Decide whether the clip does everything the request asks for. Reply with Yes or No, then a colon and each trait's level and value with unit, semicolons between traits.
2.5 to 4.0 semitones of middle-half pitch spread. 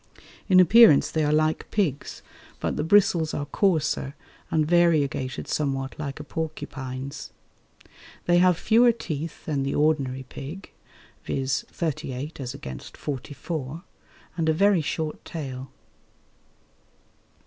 Yes: average, 3.6 semitones